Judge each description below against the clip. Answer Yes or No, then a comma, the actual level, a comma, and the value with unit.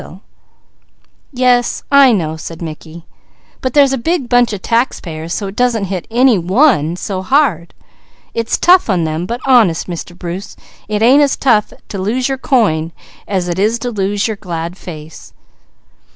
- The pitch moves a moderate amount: No, wide, 6.2 semitones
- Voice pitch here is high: Yes, high, 205 Hz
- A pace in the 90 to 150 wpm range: No, average, 170 wpm